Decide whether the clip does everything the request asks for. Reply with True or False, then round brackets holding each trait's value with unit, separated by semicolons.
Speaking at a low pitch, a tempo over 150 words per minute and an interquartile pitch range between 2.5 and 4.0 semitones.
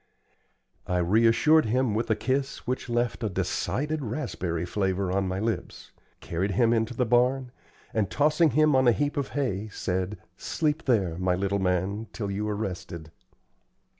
False (110 Hz; 165 wpm; 5.3 semitones)